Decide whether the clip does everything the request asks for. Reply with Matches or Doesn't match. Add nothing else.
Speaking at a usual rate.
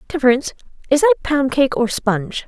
Matches